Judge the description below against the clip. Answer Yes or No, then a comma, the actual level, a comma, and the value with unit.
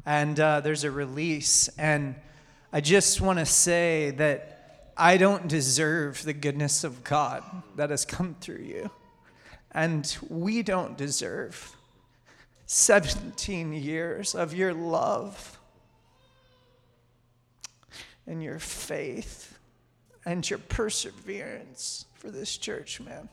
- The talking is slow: Yes, slow, 110 wpm